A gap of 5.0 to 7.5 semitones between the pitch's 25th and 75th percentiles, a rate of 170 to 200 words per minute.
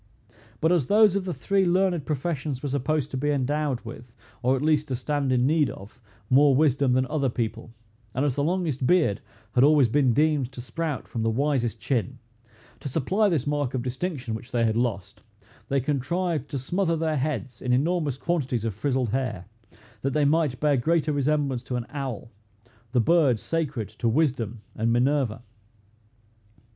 No: average, 3.9 semitones; average, 180 wpm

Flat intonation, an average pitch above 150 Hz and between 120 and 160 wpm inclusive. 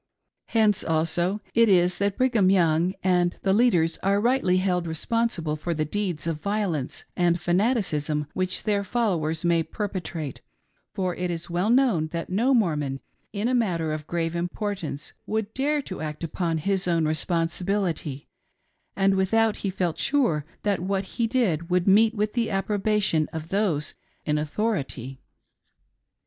No: average, 4.3 semitones; medium, 185 Hz; average, 150 wpm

